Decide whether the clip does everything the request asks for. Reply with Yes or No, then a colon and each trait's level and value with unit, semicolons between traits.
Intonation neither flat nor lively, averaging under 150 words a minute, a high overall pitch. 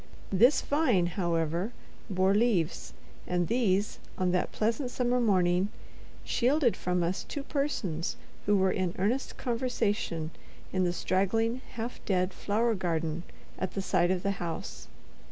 Yes: average, 4.8 semitones; slow, 135 wpm; high, 195 Hz